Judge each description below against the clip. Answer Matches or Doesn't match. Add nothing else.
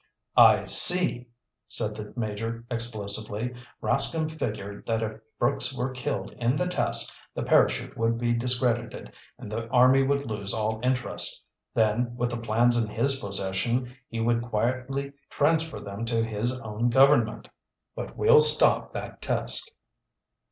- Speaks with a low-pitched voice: Matches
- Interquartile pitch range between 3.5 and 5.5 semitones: Doesn't match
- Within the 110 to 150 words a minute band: Matches